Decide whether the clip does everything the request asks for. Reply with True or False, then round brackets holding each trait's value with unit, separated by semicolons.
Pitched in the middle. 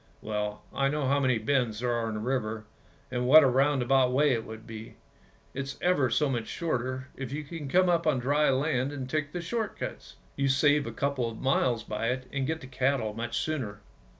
False (130 Hz)